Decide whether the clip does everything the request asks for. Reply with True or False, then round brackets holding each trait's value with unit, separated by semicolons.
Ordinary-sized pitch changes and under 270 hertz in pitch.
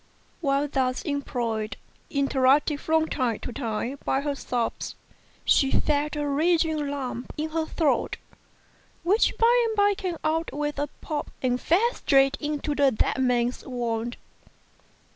False (3.7 semitones; 285 Hz)